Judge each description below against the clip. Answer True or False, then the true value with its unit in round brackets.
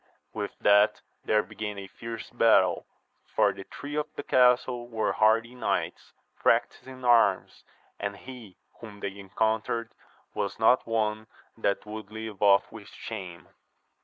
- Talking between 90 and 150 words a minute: True (140 wpm)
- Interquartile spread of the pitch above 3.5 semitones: False (2.4 semitones)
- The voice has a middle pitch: False (110 Hz)